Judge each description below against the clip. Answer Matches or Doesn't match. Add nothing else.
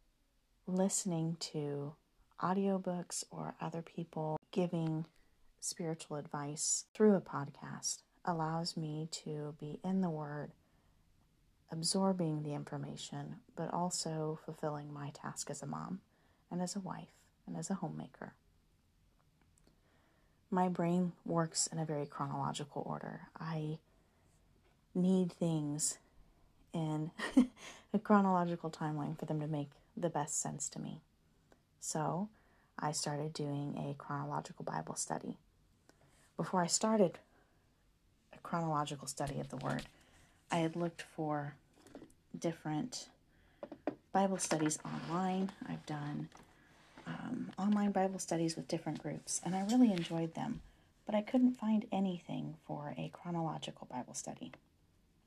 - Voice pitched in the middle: Matches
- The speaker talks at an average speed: Doesn't match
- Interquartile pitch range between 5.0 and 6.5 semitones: Doesn't match